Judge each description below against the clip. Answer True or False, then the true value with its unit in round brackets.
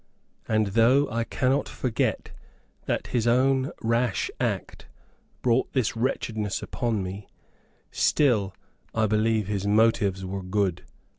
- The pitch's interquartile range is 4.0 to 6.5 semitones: False (3.3 semitones)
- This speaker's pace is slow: True (120 wpm)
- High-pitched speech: False (110 Hz)